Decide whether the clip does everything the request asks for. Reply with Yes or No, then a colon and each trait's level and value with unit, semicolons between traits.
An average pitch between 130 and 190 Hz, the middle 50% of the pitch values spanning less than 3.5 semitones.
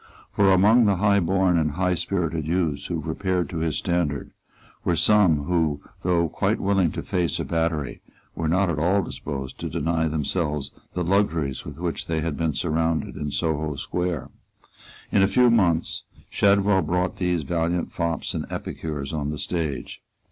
No: very low, 85 Hz; average, 3.1 semitones